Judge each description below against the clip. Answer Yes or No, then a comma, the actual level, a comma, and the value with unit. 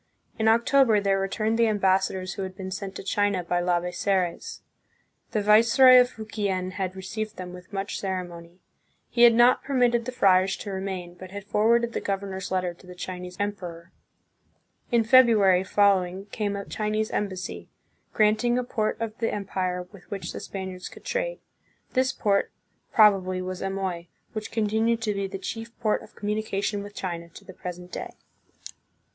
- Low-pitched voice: No, high, 200 Hz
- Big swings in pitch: No, average, 2.9 semitones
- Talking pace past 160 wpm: Yes, average, 170 wpm